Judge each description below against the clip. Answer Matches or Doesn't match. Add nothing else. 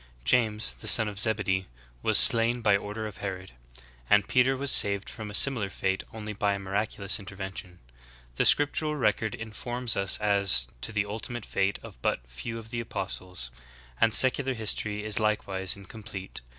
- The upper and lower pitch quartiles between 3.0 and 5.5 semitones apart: Doesn't match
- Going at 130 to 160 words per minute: Doesn't match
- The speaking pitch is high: Doesn't match